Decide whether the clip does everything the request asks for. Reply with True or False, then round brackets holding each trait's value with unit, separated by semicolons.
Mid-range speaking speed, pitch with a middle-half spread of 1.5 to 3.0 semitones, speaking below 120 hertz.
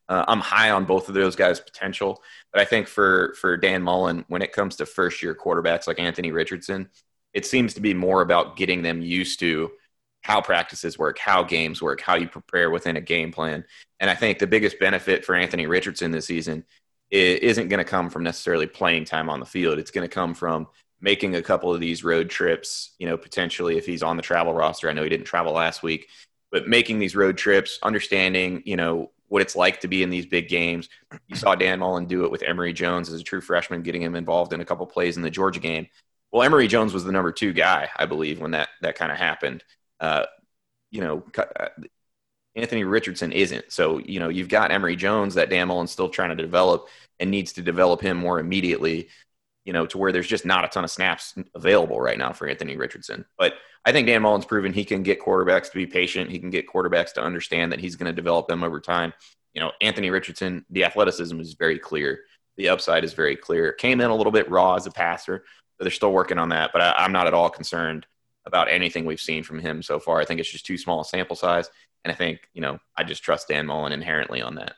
False (235 wpm; 2.5 semitones; 90 Hz)